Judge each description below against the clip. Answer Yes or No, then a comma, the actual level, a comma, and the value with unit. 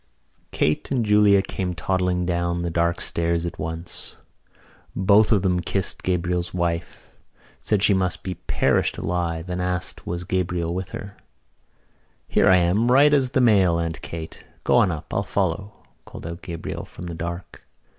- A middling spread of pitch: No, narrow, 2.3 semitones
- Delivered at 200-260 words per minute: No, average, 165 wpm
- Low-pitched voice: Yes, very low, 90 Hz